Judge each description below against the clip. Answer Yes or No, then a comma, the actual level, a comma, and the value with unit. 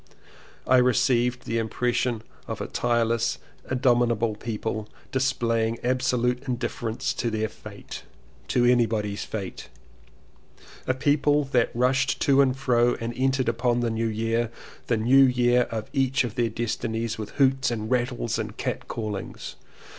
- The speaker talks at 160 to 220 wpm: No, average, 145 wpm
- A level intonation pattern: Yes, narrow, 2.0 semitones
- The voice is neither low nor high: No, low, 120 Hz